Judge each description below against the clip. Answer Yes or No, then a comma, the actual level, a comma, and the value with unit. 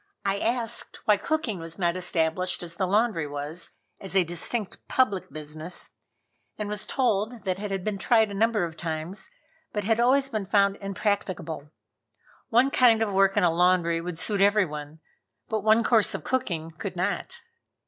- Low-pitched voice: No, high, 195 Hz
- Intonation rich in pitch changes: No, average, 4.3 semitones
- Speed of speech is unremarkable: Yes, average, 170 wpm